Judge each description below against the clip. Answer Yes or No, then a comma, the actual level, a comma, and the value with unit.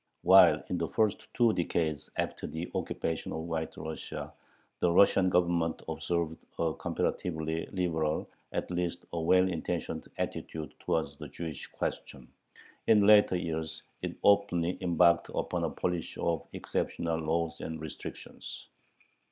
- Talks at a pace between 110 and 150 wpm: Yes, slow, 135 wpm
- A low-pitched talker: Yes, very low, 85 Hz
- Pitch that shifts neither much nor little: No, narrow, 1.8 semitones